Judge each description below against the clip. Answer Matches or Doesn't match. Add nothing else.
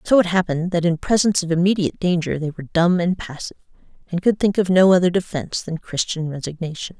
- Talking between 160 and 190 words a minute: Doesn't match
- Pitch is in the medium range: Matches